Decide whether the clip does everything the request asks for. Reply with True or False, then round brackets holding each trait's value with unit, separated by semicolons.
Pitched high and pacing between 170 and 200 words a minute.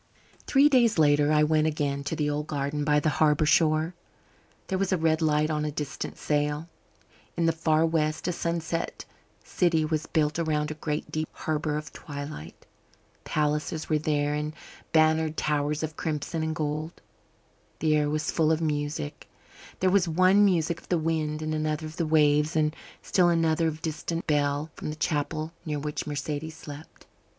False (155 Hz; 175 wpm)